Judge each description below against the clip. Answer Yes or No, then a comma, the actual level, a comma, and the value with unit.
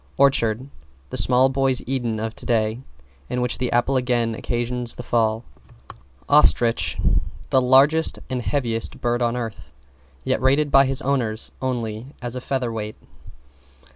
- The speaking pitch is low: Yes, low, 125 Hz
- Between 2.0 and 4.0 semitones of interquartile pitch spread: Yes, narrow, 2.4 semitones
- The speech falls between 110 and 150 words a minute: Yes, average, 140 wpm